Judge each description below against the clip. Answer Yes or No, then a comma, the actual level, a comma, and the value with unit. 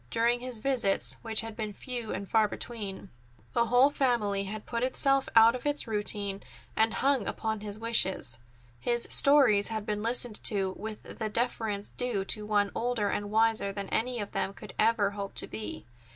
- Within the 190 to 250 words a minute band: No, average, 180 wpm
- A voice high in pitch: Yes, high, 220 Hz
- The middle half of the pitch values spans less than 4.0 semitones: Yes, average, 2.8 semitones